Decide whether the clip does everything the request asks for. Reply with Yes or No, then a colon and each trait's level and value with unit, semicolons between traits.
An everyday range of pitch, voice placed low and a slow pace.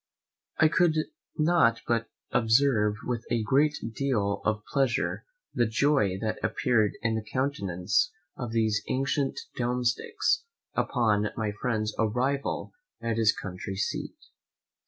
Yes: average, 4.0 semitones; low, 115 Hz; slow, 120 wpm